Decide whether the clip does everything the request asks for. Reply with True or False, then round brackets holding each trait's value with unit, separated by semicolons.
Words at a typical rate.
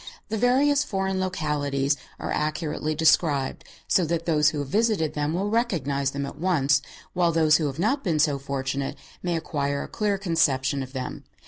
True (180 wpm)